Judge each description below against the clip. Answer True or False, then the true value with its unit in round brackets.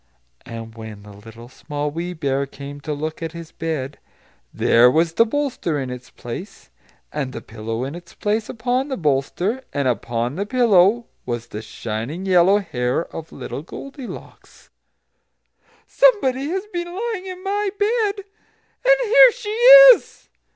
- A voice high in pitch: False (170 Hz)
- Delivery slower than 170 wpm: True (150 wpm)